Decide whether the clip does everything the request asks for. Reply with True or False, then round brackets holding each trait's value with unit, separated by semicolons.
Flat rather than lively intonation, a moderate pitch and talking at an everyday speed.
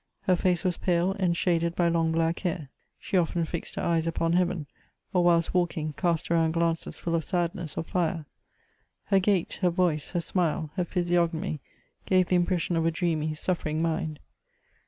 True (1.6 semitones; 170 Hz; 180 wpm)